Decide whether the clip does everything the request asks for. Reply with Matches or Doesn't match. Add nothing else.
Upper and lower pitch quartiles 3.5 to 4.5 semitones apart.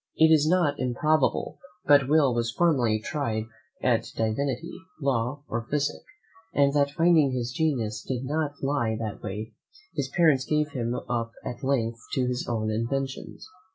Matches